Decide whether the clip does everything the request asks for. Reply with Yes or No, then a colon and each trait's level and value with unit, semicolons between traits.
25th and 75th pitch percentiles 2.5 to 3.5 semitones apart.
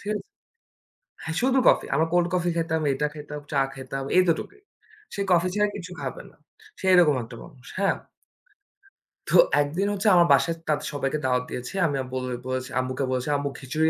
No: average, 4.8 semitones